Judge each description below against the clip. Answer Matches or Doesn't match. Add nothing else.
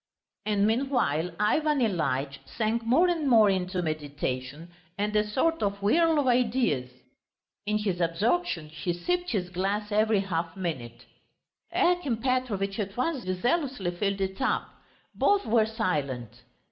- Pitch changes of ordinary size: Doesn't match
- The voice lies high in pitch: Matches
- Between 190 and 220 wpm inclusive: Doesn't match